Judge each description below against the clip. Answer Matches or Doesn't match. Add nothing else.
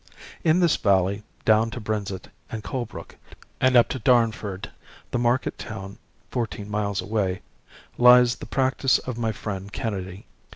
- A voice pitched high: Doesn't match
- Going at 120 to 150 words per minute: Matches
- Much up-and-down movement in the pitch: Doesn't match